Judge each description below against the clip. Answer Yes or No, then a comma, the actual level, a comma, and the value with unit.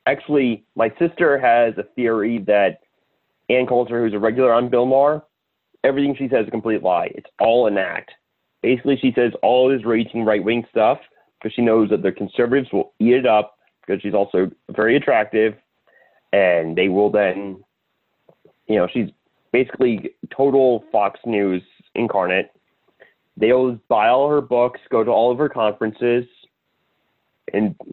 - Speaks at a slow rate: No, average, 160 wpm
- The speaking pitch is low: Yes, low, 115 Hz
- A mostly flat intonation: No, average, 3.2 semitones